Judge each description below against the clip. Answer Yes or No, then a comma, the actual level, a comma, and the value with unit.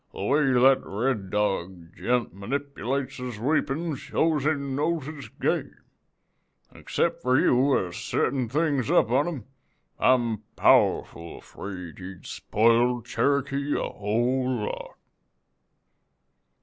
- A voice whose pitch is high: No, low, 125 Hz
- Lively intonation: No, average, 4.8 semitones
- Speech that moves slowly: Yes, slow, 120 wpm